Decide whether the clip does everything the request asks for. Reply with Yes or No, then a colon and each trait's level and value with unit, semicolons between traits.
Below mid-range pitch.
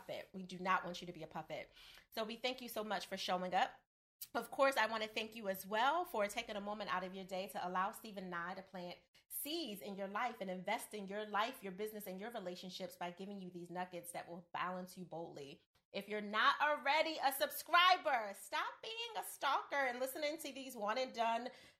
No: high, 205 Hz